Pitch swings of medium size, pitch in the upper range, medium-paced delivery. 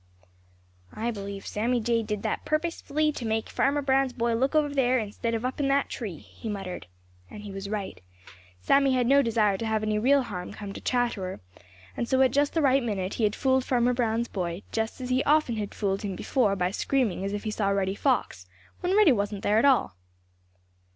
No: average, 4.6 semitones; high, 230 Hz; fast, 210 wpm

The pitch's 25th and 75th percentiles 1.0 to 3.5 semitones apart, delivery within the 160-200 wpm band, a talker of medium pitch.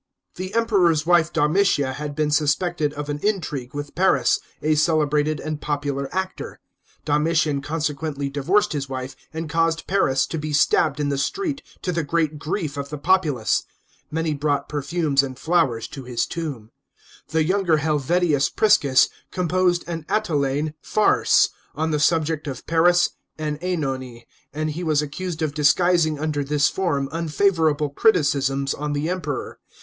No: average, 3.0 semitones; average, 150 wpm; medium, 155 Hz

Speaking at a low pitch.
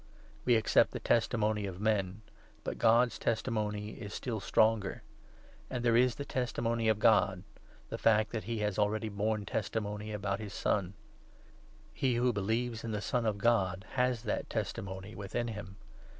Yes: low, 110 Hz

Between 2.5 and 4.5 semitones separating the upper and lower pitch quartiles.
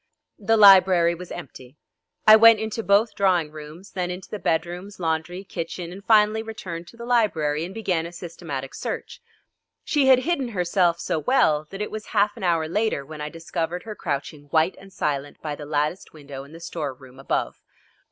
No: average, 5.0 semitones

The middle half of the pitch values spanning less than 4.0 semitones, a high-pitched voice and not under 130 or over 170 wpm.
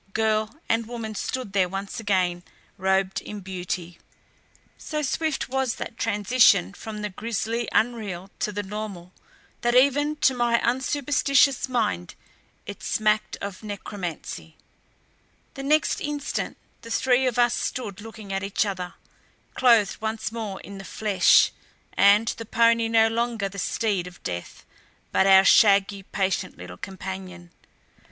Yes: average, 3.6 semitones; high, 215 Hz; average, 140 wpm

